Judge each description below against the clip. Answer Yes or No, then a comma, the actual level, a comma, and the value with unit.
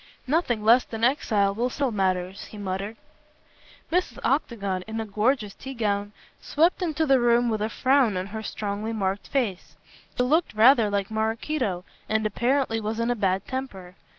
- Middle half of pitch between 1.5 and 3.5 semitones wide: No, average, 4.1 semitones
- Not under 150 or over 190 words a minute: Yes, average, 170 wpm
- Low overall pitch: No, high, 220 Hz